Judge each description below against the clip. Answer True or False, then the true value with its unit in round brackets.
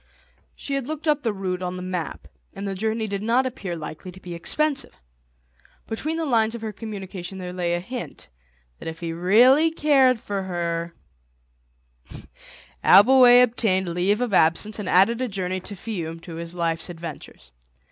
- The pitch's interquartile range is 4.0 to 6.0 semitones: True (5.4 semitones)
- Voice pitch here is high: True (195 Hz)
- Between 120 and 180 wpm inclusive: True (170 wpm)